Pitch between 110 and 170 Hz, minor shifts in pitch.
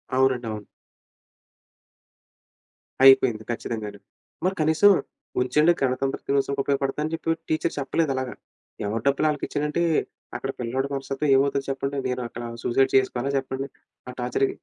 Yes: low, 135 Hz; narrow, 2.0 semitones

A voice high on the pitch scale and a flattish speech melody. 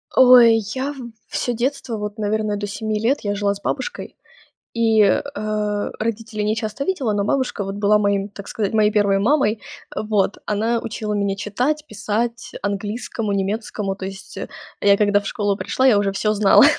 Yes: high, 210 Hz; narrow, 2.2 semitones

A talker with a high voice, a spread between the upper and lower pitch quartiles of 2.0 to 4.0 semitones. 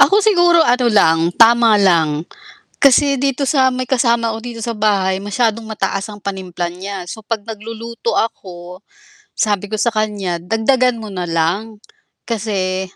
Yes: high, 215 Hz; average, 3.7 semitones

